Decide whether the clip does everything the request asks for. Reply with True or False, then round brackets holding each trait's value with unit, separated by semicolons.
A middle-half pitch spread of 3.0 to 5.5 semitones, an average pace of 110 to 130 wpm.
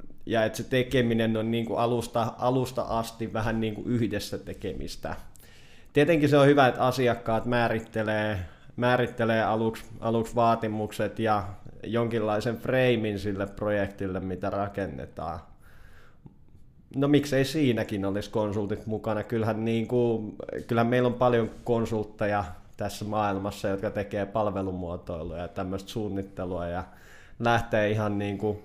False (2.4 semitones; 125 wpm)